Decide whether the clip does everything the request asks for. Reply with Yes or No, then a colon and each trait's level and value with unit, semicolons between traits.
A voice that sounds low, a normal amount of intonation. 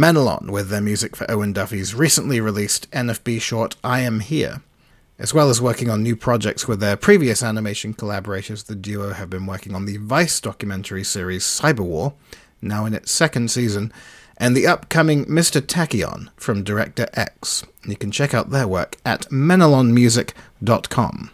Yes: low, 115 Hz; average, 3.6 semitones